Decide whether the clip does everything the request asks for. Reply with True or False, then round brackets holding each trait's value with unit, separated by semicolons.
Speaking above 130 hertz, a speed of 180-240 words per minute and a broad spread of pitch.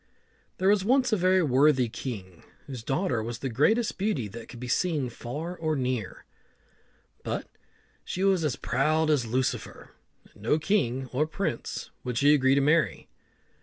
False (140 Hz; 165 wpm; 5.8 semitones)